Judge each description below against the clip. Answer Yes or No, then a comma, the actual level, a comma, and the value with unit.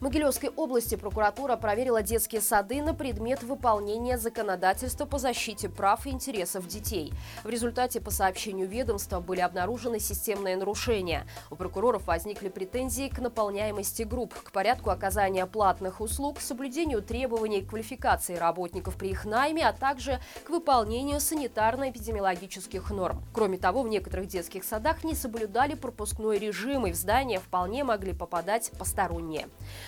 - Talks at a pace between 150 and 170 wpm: No, average, 140 wpm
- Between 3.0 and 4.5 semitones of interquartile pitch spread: No, average, 5.0 semitones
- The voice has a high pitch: Yes, high, 225 Hz